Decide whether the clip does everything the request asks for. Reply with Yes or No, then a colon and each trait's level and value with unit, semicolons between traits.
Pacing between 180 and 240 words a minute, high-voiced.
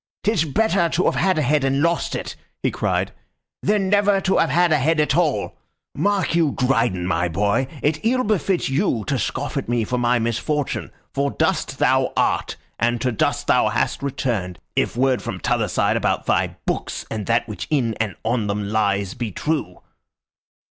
No: average, 190 wpm; low, 135 Hz